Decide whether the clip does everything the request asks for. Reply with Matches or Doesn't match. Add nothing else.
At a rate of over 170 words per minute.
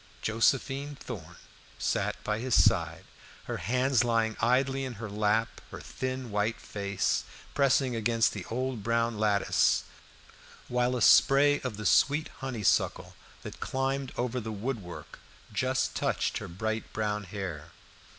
Doesn't match